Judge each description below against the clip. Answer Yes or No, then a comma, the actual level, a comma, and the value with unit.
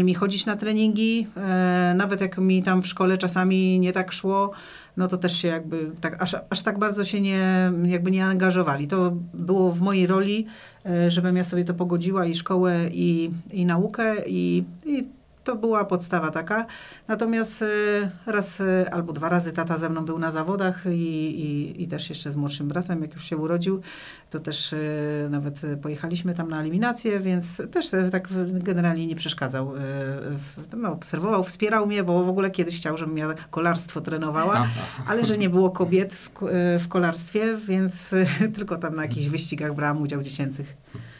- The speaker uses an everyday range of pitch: Yes, average, 3.1 semitones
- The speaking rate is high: Yes, fast, 170 wpm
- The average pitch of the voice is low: No, medium, 180 Hz